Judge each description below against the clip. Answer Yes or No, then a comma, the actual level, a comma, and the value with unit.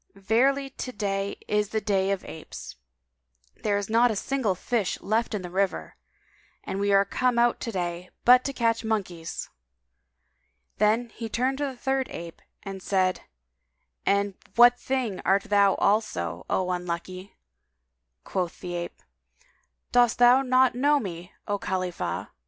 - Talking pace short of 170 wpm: Yes, average, 150 wpm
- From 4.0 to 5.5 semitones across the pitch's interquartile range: Yes, average, 4.6 semitones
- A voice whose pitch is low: No, high, 205 Hz